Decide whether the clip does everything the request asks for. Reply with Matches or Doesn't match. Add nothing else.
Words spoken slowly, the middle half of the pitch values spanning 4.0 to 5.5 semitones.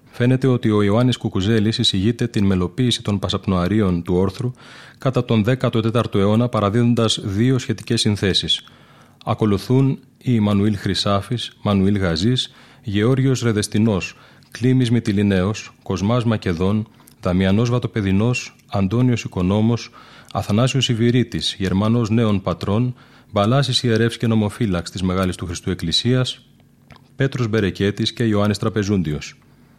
Doesn't match